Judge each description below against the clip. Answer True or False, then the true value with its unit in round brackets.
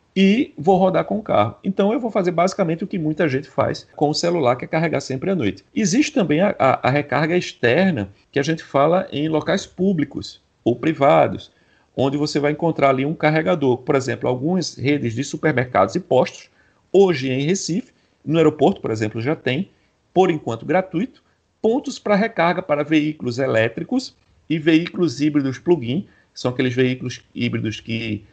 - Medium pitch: True (155 Hz)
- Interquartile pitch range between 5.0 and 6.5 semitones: True (5.6 semitones)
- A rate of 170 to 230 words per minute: True (180 wpm)